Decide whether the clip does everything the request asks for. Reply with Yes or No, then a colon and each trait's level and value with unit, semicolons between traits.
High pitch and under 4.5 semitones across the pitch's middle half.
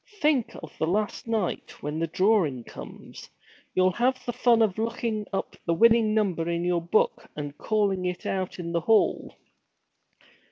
No: high, 195 Hz; average, 4.8 semitones